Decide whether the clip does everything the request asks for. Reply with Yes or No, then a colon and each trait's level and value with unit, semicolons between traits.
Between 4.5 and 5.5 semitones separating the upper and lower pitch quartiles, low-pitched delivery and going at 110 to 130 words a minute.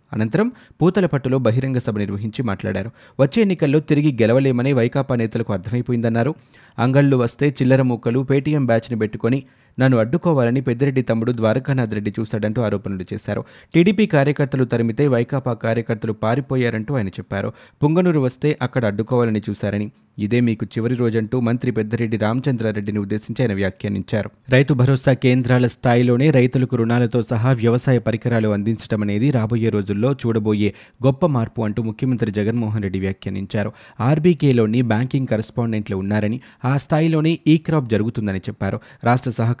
No: average, 3.5 semitones; low, 120 Hz; fast, 125 wpm